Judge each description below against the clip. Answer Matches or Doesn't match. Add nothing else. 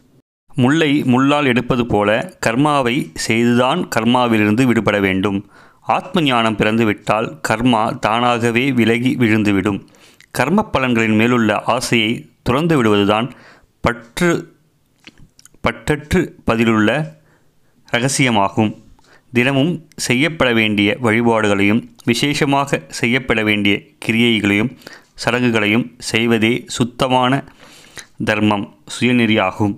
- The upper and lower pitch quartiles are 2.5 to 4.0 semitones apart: Matches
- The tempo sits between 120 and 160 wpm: Doesn't match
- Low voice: Matches